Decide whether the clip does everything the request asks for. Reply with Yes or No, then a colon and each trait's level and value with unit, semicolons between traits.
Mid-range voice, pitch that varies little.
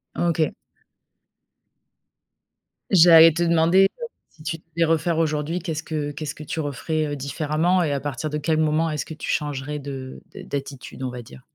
Yes: medium, 155 Hz; narrow, 2.2 semitones